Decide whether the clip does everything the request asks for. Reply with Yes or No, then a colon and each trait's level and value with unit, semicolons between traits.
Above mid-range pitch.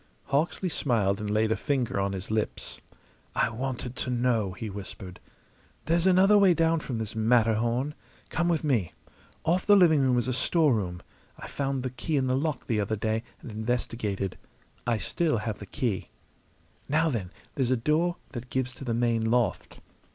No: low, 125 Hz